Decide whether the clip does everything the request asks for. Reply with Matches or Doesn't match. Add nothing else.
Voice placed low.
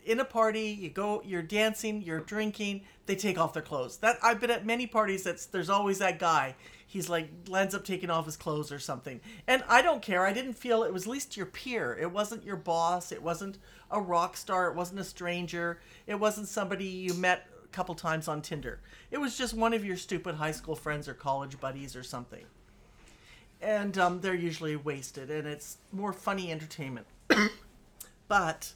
Doesn't match